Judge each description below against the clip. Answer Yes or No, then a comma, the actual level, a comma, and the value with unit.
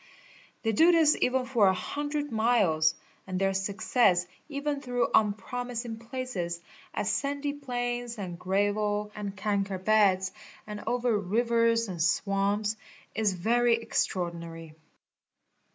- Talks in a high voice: Yes, high, 215 Hz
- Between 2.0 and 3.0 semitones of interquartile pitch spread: No, average, 4.1 semitones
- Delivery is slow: Yes, slow, 120 wpm